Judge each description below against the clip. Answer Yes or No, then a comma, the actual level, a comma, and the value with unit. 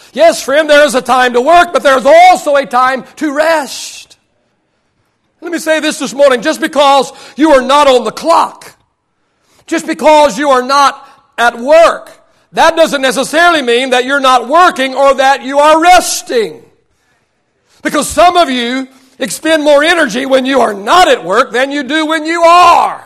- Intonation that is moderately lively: Yes, average, 3.4 semitones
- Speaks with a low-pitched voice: No, very high, 285 Hz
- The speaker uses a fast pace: No, average, 180 wpm